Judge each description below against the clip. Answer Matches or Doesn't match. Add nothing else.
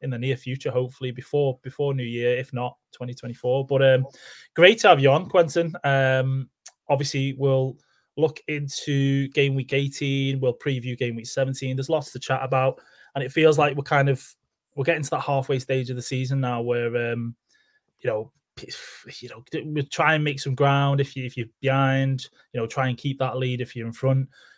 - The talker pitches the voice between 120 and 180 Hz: Matches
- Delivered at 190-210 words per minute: Matches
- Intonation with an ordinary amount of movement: Doesn't match